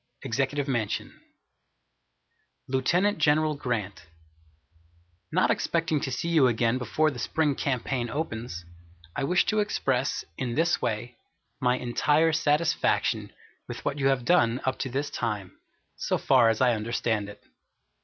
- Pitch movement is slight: No, average, 4.4 semitones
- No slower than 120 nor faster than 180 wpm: Yes, slow, 135 wpm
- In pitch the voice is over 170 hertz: No, low, 130 Hz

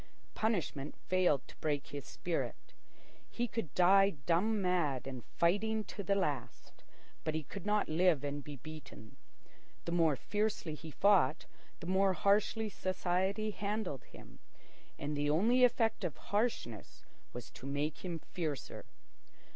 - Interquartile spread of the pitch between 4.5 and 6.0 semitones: Yes, wide, 5.6 semitones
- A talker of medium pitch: Yes, medium, 175 Hz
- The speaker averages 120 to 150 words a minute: Yes, average, 140 wpm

